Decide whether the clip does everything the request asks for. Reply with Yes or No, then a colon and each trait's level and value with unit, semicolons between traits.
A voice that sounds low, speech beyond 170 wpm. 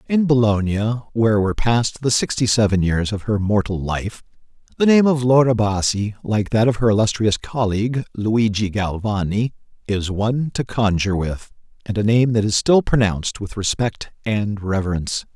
No: low, 110 Hz; average, 165 wpm